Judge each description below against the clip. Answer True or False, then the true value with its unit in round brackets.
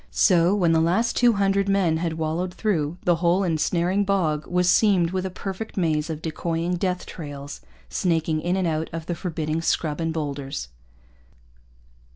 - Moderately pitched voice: True (170 Hz)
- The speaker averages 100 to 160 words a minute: False (170 wpm)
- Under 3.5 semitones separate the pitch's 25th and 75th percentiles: True (2.7 semitones)